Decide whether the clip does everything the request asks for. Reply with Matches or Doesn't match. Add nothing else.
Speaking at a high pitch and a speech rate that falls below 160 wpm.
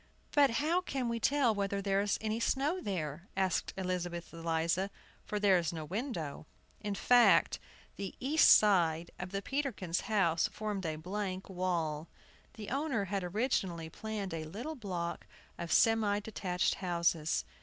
Matches